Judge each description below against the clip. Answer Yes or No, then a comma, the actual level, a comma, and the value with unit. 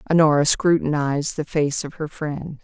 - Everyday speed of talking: Yes, average, 160 wpm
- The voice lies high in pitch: No, medium, 150 Hz